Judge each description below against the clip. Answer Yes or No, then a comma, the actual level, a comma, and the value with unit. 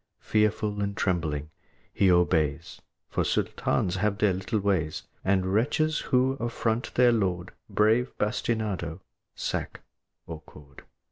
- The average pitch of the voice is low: Yes, low, 100 Hz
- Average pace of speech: No, slow, 120 wpm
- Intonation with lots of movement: No, average, 4.0 semitones